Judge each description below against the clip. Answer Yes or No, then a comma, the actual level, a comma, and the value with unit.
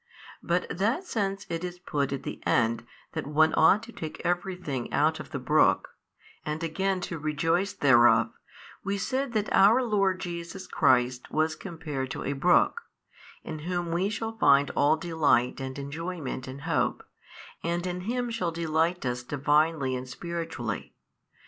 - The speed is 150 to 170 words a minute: Yes, average, 160 wpm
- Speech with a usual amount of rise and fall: Yes, average, 4.8 semitones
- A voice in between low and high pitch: Yes, medium, 165 Hz